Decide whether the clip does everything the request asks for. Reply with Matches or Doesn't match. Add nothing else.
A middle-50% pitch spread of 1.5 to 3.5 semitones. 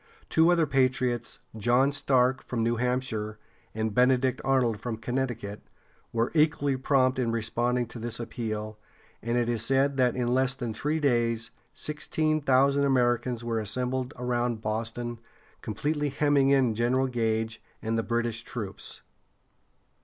Matches